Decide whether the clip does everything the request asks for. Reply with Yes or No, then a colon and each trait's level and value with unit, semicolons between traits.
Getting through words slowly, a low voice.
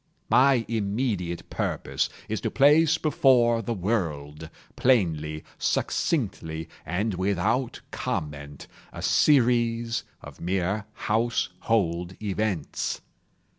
Yes: slow, 90 wpm; low, 105 Hz